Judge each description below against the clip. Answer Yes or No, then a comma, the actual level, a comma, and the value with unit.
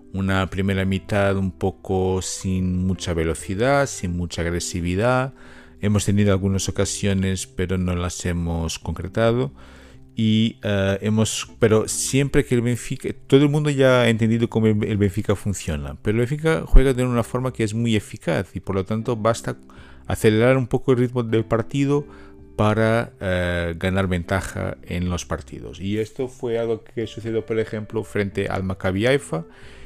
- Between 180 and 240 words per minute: No, average, 160 wpm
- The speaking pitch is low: Yes, low, 100 Hz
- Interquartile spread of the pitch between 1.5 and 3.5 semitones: No, average, 3.9 semitones